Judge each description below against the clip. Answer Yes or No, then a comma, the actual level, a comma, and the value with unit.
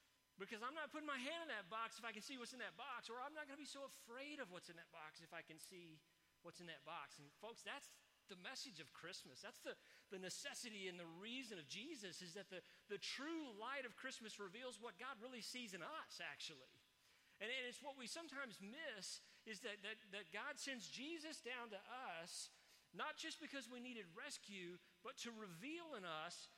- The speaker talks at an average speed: No, fast, 220 wpm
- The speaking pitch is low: No, high, 235 Hz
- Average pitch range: No, wide, 5.9 semitones